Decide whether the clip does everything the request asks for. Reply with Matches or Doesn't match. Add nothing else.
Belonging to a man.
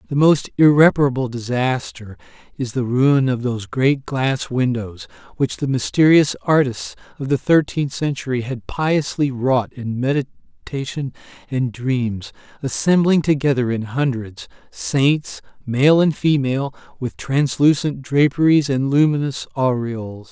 Matches